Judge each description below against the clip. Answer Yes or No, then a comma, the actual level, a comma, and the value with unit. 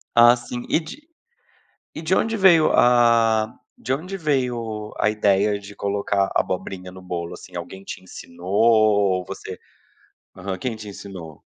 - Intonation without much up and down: No, average, 4.2 semitones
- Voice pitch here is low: Yes, low, 105 Hz